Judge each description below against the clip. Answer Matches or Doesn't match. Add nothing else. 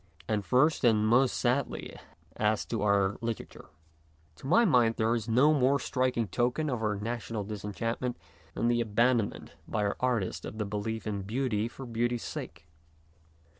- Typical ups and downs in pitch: Matches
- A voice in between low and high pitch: Doesn't match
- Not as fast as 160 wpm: Doesn't match